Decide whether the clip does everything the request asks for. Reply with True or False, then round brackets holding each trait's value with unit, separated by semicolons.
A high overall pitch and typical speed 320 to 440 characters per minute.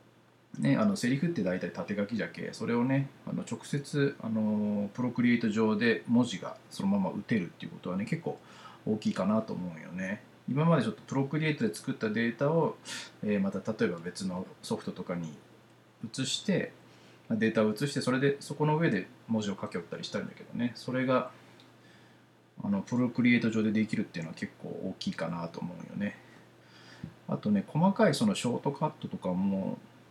False (130 Hz; 350 characters per minute)